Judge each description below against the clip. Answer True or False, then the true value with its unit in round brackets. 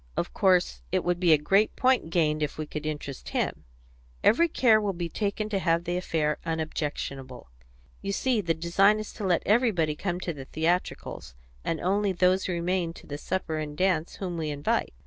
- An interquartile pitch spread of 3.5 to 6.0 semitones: True (4.0 semitones)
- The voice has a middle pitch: True (175 Hz)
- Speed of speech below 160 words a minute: False (190 wpm)